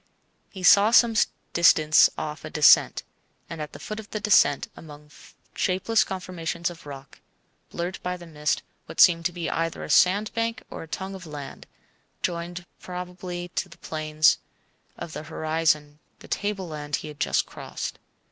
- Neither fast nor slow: Yes, average, 160 wpm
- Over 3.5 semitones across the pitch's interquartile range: No, average, 3.2 semitones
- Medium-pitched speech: Yes, medium, 170 Hz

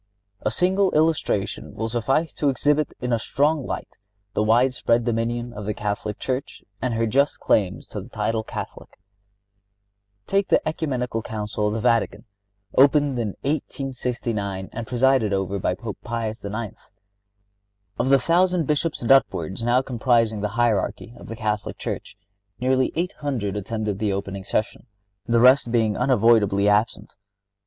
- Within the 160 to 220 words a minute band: No, average, 150 wpm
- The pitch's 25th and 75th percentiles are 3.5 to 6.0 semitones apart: Yes, average, 4.0 semitones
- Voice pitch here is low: Yes, low, 115 Hz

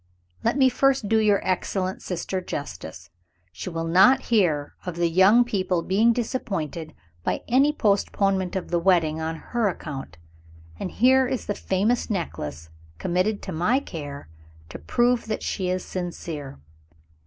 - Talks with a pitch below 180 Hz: No, medium, 185 Hz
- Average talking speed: Yes, average, 150 wpm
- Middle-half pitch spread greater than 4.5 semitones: Yes, wide, 5.5 semitones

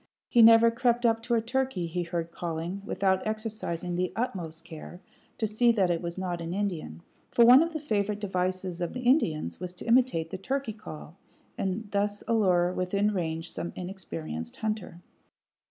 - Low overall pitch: No, high, 190 Hz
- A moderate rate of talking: Yes, average, 175 wpm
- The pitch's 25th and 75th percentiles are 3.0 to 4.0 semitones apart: No, average, 4.7 semitones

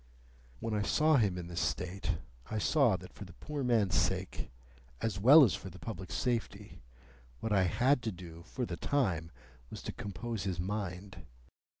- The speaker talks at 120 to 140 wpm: No, average, 180 wpm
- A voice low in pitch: Yes, low, 100 Hz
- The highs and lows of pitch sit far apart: No, average, 4.6 semitones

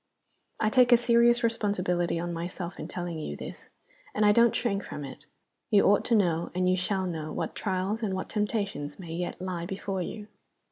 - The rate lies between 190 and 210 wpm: Yes, average, 195 wpm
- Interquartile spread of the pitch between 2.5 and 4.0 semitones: Yes, average, 3.6 semitones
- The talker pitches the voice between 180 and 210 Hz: Yes, high, 190 Hz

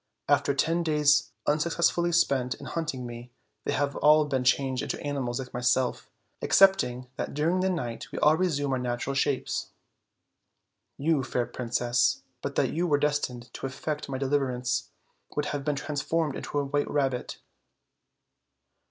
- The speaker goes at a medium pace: Yes, average, 155 wpm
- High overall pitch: No, medium, 140 Hz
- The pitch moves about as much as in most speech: Yes, average, 3.1 semitones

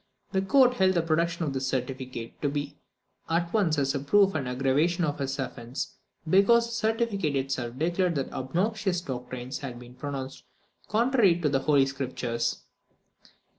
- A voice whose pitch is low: No, medium, 145 Hz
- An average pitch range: No, wide, 6.1 semitones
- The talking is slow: No, average, 165 wpm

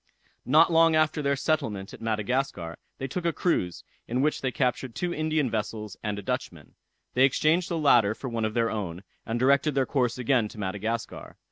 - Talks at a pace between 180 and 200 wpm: Yes, average, 195 wpm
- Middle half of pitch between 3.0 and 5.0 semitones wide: No, wide, 5.6 semitones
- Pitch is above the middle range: No, low, 125 Hz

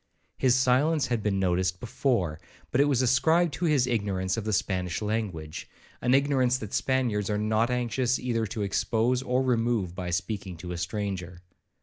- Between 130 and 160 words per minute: No, average, 170 wpm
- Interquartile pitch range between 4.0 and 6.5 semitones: Yes, average, 5.2 semitones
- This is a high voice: No, low, 110 Hz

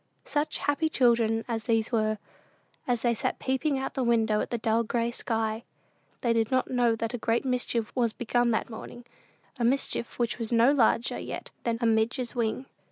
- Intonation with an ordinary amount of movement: No, narrow, 1.8 semitones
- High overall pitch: Yes, high, 235 Hz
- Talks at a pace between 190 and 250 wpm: Yes, average, 195 wpm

